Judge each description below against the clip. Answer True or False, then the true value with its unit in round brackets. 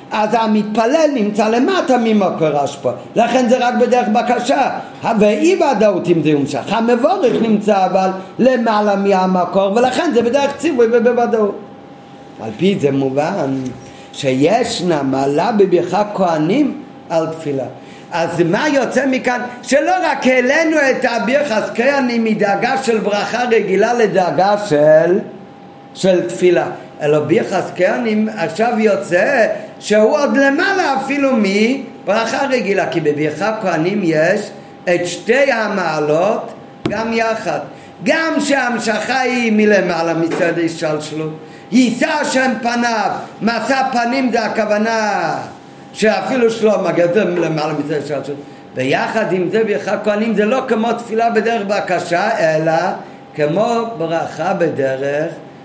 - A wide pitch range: True (6.1 semitones)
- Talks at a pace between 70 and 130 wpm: True (120 wpm)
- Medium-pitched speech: False (210 Hz)